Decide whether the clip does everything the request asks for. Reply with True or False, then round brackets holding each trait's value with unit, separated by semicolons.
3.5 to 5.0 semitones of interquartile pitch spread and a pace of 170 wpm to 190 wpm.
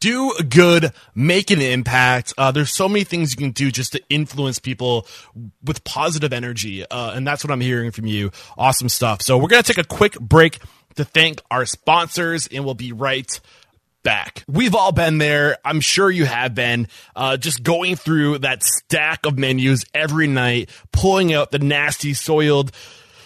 True (4.2 semitones; 185 wpm)